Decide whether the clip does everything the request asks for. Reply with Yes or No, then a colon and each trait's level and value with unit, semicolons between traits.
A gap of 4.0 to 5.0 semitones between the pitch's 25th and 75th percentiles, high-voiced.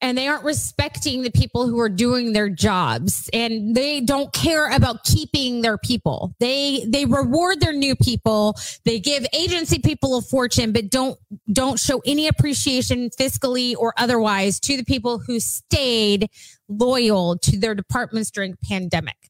No: average, 3.5 semitones; high, 245 Hz